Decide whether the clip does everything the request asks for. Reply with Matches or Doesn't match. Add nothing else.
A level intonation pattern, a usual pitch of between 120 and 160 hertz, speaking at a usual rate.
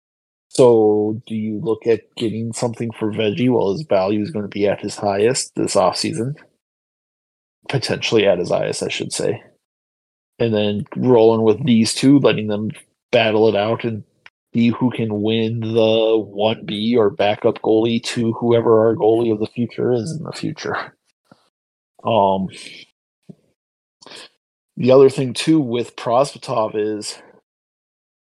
Doesn't match